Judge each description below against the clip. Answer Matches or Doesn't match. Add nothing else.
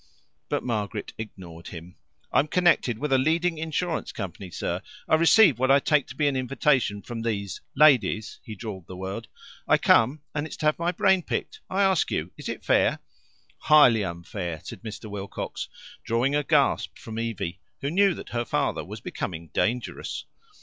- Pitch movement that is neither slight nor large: Doesn't match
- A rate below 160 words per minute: Doesn't match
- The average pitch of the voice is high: Doesn't match